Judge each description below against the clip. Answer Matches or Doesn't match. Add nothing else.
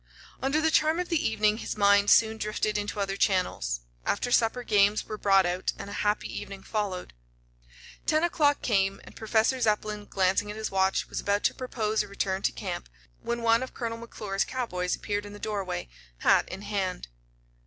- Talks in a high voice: Matches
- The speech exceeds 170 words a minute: Matches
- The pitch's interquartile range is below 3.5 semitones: Matches